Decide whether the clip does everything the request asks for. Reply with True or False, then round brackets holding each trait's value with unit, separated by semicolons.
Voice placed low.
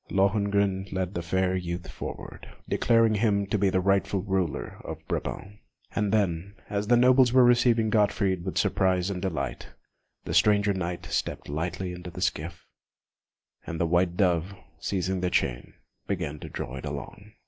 True (95 Hz)